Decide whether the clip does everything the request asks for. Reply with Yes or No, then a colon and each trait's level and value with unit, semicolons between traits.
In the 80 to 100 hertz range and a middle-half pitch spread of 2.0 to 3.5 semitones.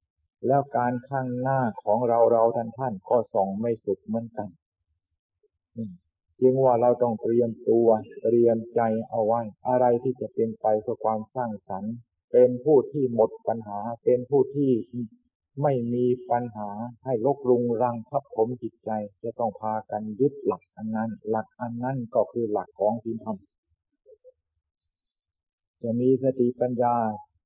No: low, 115 Hz; narrow, 2.5 semitones